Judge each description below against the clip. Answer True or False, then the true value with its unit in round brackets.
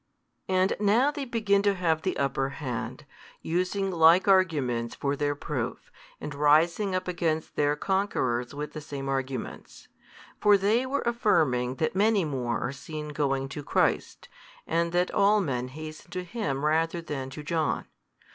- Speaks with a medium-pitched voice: True (160 Hz)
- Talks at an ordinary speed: True (155 wpm)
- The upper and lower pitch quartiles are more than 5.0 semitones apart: True (5.6 semitones)